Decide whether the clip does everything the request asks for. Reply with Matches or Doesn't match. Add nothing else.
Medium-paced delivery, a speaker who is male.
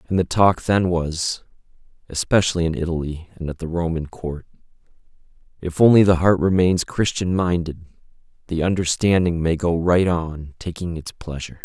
Matches